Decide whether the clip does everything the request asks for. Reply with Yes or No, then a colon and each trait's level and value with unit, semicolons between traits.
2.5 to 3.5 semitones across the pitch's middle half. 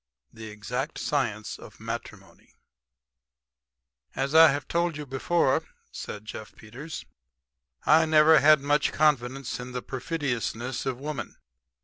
No: average, 3.9 semitones